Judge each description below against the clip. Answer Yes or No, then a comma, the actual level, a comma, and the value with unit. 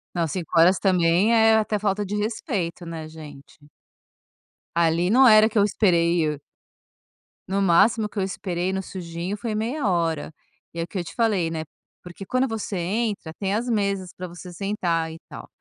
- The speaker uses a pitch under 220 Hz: Yes, high, 190 Hz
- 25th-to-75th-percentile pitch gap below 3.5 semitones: No, average, 3.9 semitones